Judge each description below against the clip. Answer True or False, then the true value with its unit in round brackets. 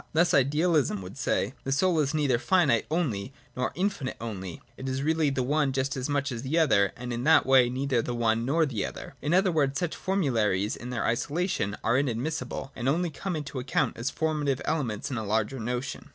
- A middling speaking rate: False (215 wpm)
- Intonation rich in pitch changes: False (4.5 semitones)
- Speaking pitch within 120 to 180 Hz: True (135 Hz)